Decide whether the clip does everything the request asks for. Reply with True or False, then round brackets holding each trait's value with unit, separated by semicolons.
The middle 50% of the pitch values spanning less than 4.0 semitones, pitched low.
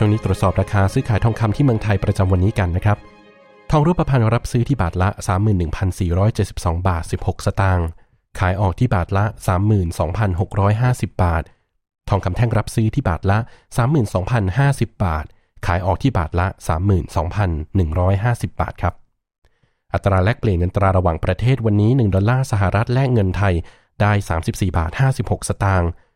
True (3.4 semitones; 100 Hz)